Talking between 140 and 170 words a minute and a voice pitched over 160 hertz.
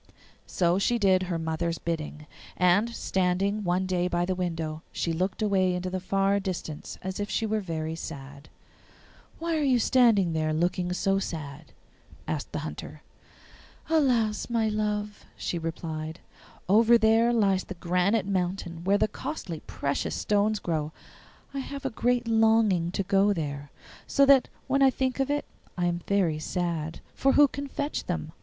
Yes: average, 165 wpm; high, 190 Hz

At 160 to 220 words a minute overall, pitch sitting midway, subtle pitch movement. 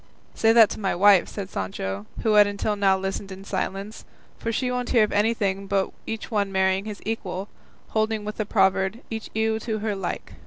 No: average, 200 wpm; high, 205 Hz; narrow, 2.3 semitones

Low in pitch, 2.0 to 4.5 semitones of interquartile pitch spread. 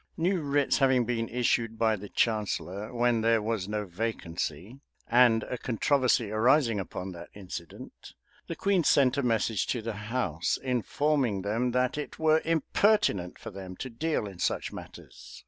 Yes: low, 115 Hz; average, 4.1 semitones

